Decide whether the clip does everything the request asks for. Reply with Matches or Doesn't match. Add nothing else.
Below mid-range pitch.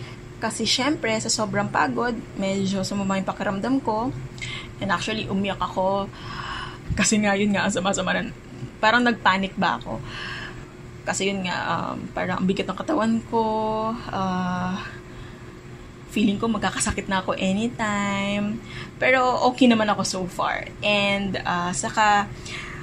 Doesn't match